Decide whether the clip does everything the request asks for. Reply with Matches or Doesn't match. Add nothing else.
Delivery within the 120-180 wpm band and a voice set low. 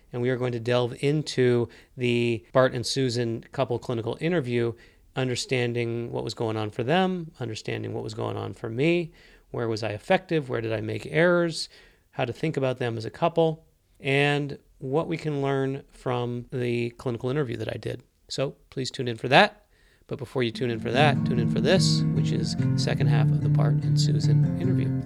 Doesn't match